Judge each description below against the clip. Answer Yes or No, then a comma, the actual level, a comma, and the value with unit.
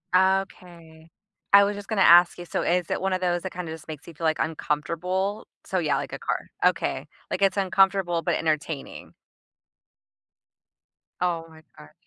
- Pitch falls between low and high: Yes, medium, 175 Hz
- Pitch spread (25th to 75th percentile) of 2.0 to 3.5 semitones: Yes, average, 2.9 semitones